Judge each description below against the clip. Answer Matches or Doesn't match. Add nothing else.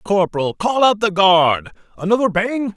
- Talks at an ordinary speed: Matches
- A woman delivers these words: Doesn't match